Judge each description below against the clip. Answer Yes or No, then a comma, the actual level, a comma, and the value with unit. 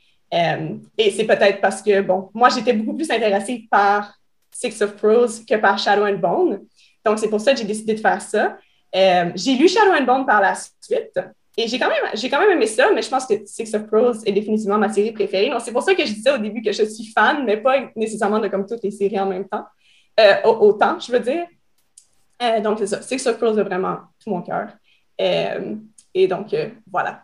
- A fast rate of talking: Yes, fast, 235 wpm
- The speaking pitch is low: No, high, 220 Hz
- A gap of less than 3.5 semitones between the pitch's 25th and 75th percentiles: No, average, 3.9 semitones